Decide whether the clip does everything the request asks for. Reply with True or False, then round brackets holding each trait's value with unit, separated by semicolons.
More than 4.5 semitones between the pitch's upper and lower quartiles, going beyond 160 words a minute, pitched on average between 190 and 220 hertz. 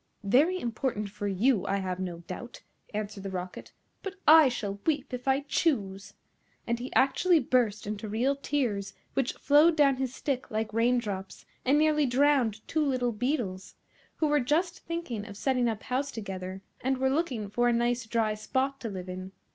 False (5.2 semitones; 180 wpm; 240 Hz)